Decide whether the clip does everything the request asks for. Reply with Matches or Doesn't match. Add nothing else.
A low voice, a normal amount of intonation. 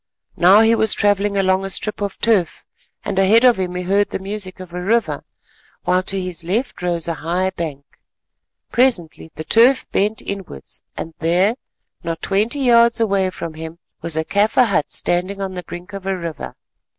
Doesn't match